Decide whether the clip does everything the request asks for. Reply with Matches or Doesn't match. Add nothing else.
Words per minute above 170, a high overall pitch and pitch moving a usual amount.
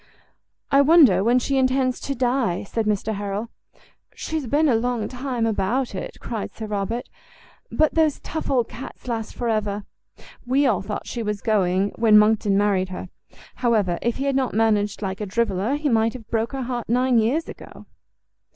Matches